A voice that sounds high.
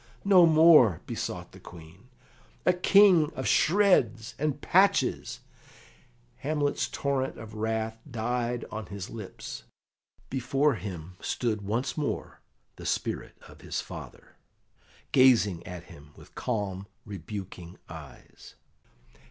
No: low, 115 Hz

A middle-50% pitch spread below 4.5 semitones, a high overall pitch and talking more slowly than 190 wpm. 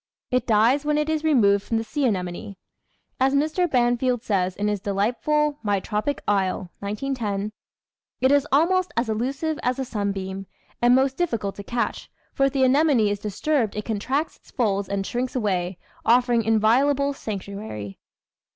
No: average, 5.3 semitones; high, 235 Hz; average, 165 wpm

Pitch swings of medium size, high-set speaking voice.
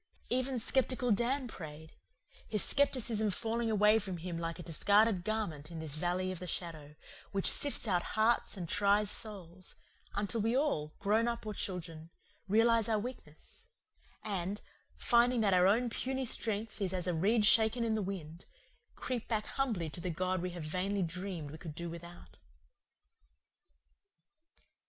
Yes: average, 4.7 semitones; high, 200 Hz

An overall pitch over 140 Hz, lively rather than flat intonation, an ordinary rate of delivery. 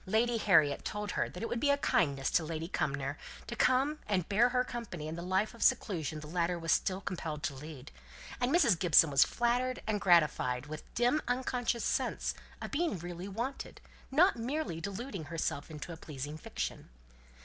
Yes: medium, 185 Hz; wide, 7.4 semitones; average, 190 wpm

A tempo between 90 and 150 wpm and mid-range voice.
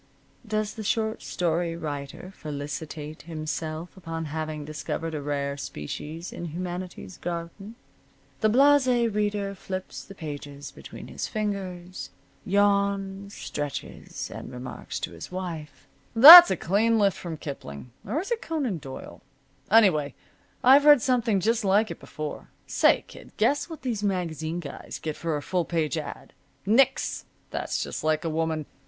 Yes: average, 145 wpm; medium, 175 Hz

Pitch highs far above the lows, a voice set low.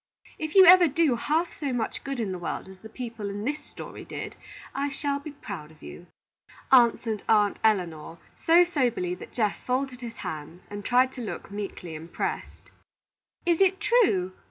No: wide, 6.8 semitones; high, 235 Hz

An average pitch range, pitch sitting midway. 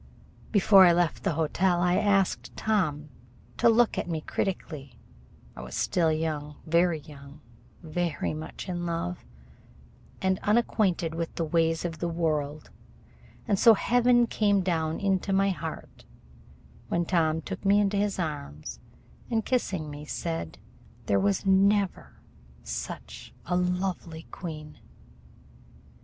Yes: average, 3.7 semitones; medium, 175 Hz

